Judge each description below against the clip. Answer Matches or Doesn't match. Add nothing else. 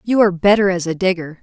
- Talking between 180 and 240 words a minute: Doesn't match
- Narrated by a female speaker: Matches